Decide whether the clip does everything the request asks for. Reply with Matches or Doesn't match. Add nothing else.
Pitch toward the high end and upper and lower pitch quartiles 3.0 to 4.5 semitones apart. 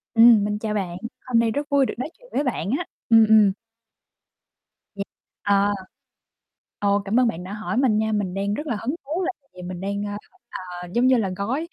Matches